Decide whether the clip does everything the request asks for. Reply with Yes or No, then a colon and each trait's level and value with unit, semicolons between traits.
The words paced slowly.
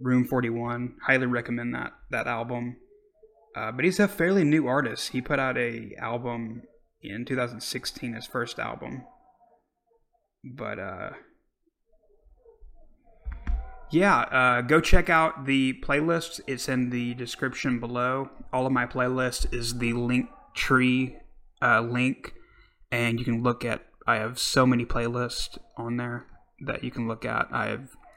No: average, 145 wpm